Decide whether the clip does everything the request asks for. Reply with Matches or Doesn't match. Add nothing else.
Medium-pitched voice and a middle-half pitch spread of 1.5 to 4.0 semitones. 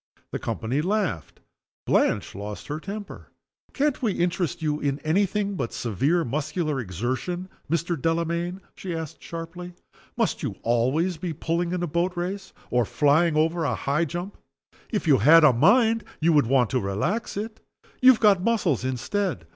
Doesn't match